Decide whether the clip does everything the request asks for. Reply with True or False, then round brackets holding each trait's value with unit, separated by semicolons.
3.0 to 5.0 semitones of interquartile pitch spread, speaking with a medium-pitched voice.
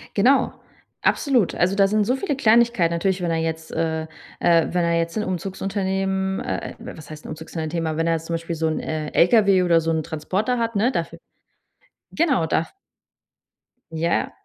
True (3.9 semitones; 175 Hz)